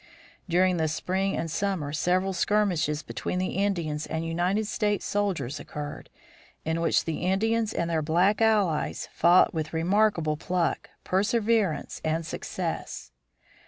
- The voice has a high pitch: No, medium, 180 Hz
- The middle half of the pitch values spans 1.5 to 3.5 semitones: No, average, 4.1 semitones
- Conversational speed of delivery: No, slow, 130 wpm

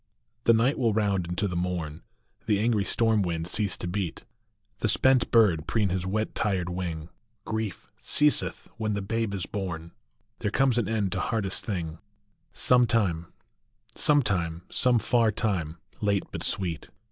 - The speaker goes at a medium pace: Yes, average, 160 wpm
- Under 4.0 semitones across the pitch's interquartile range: No, average, 4.3 semitones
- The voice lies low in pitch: Yes, low, 100 Hz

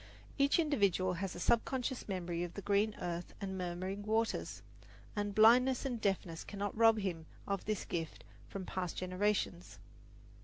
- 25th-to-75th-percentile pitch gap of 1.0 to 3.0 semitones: No, average, 3.4 semitones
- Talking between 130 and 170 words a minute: Yes, average, 150 wpm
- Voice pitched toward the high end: Yes, high, 200 Hz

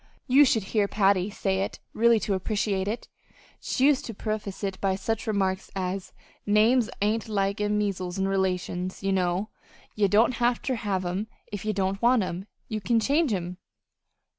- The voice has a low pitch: No, high, 205 Hz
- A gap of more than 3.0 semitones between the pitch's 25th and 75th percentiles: No, average, 2.7 semitones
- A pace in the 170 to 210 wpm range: Yes, average, 180 wpm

